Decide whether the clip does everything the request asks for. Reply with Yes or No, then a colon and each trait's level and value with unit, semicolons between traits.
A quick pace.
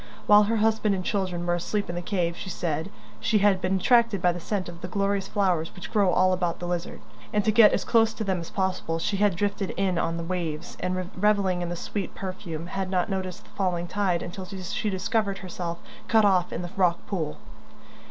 Yes: fast, 220 wpm